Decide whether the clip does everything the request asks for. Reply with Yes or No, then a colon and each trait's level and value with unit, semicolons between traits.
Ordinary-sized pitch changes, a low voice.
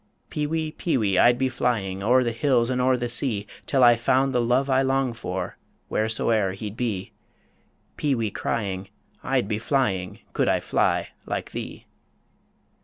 Yes: average, 3.8 semitones; low, 120 Hz